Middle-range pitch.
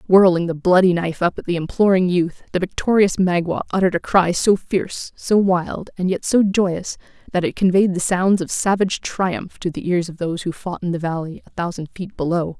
Yes: medium, 180 Hz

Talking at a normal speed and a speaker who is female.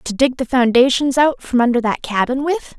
No: fast, 215 wpm; female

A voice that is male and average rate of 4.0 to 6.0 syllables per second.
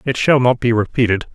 Yes: male; 5.8 syllables/s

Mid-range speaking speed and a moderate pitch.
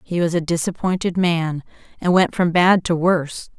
Yes: average, 185 wpm; medium, 170 Hz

